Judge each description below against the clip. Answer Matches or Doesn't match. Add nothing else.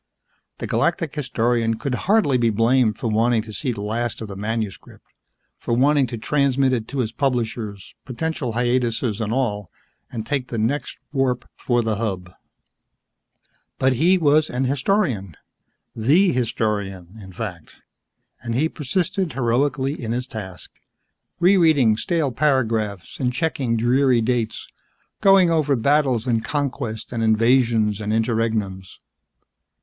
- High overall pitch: Doesn't match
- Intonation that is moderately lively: Matches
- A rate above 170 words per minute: Doesn't match